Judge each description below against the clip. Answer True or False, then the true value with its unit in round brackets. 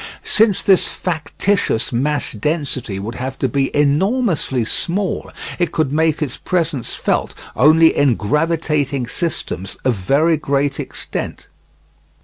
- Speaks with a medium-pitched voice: True (145 Hz)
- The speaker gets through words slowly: True (125 wpm)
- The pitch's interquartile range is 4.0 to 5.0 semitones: True (4.3 semitones)